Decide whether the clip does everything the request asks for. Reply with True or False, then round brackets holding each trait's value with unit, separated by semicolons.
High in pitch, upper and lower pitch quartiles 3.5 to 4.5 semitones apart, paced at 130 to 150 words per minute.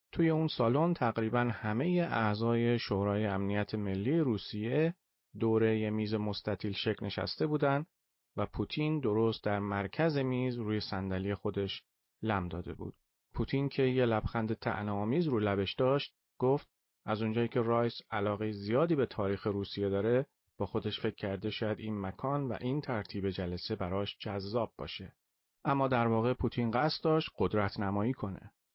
False (110 Hz; 3.8 semitones; 145 wpm)